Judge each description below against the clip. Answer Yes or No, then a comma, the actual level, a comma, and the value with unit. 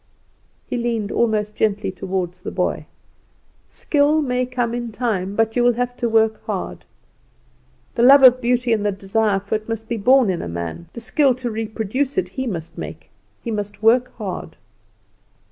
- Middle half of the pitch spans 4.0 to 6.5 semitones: No, average, 3.6 semitones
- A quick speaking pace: No, average, 180 wpm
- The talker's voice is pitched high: Yes, high, 225 Hz